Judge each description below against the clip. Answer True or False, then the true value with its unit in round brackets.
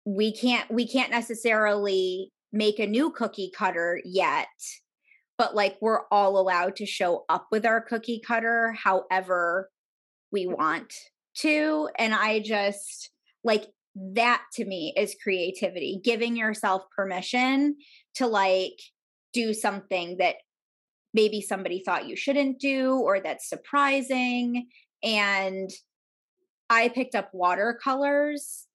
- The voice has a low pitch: False (220 Hz)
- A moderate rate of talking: False (120 wpm)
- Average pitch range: True (4.3 semitones)